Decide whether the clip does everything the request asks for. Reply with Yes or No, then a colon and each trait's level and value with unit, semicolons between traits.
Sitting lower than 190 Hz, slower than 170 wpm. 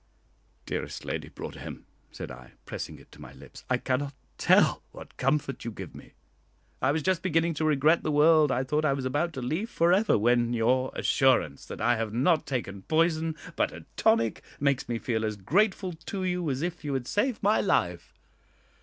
No: medium, 140 Hz; average, 195 wpm